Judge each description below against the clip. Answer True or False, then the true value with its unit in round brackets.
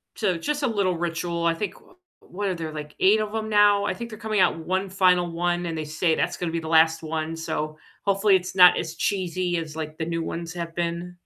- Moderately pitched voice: True (175 Hz)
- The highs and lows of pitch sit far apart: False (3.0 semitones)